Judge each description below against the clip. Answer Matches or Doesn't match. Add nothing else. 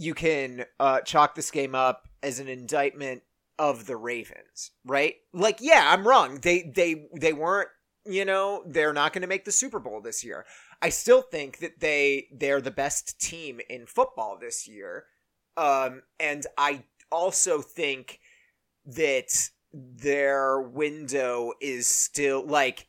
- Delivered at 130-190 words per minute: Matches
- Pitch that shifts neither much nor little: Doesn't match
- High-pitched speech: Doesn't match